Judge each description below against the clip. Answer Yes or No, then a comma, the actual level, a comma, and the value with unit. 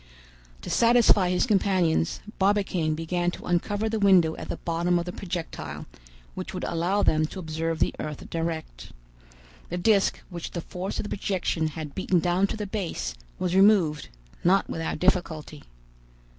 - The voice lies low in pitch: No, medium, 175 Hz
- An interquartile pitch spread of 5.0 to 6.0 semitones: No, average, 3.1 semitones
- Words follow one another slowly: No, average, 160 wpm